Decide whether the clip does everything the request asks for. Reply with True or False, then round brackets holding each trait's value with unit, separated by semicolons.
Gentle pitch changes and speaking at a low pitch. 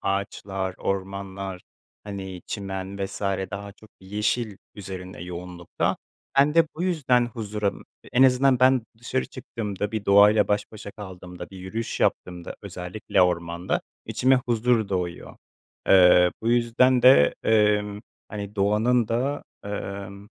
False (3.5 semitones; 100 Hz)